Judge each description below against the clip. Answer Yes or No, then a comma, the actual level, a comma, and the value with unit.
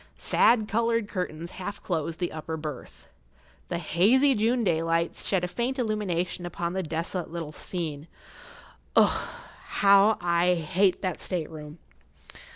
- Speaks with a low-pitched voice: No, medium, 180 Hz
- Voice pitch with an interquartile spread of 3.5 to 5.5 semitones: Yes, average, 3.8 semitones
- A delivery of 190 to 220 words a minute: No, slow, 135 wpm